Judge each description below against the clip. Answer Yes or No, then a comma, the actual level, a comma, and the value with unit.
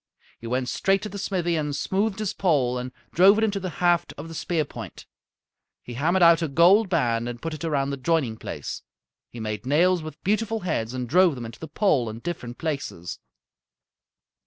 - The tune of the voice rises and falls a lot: Yes, wide, 6.5 semitones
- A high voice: No, medium, 160 Hz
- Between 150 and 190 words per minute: No, average, 200 wpm